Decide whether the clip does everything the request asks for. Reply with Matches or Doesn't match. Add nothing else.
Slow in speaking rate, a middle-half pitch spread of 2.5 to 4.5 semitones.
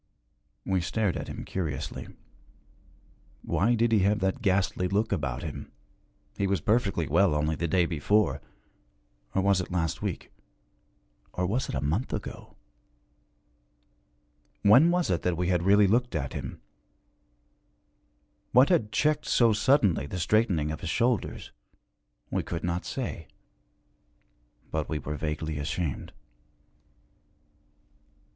Doesn't match